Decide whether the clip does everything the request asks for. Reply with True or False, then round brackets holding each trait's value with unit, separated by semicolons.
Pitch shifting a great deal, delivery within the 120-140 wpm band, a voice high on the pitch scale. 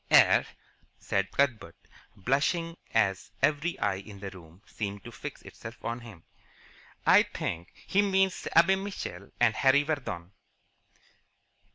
False (8.4 semitones; 135 wpm; 120 Hz)